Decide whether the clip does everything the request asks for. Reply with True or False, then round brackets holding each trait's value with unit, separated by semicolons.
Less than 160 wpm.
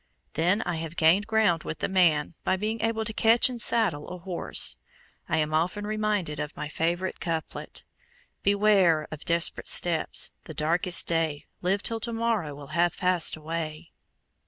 False (165 wpm)